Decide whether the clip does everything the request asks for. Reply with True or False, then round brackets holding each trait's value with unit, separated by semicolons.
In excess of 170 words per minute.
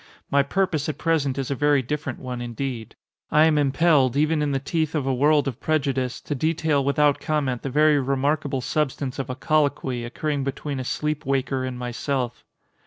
True (185 wpm)